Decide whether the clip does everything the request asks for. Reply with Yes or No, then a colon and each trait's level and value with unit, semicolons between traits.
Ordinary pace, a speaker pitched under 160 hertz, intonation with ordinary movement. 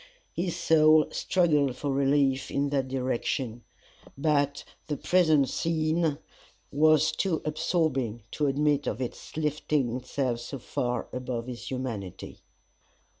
No: slow, 120 wpm; medium, 140 Hz; average, 3.4 semitones